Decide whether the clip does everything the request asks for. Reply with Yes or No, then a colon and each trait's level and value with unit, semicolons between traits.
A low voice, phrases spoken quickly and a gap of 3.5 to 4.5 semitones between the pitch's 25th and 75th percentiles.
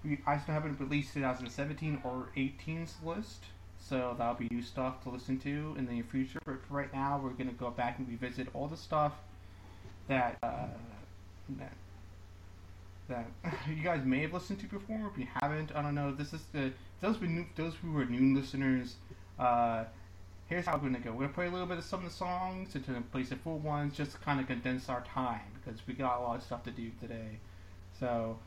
Yes: low, 130 Hz; fast, 215 wpm; average, 4.0 semitones